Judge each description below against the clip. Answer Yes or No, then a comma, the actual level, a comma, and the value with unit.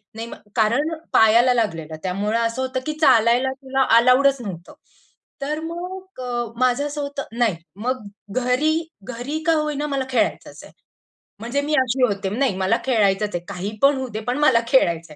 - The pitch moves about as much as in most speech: Yes, average, 4.5 semitones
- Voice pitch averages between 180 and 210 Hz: No, very high, 250 Hz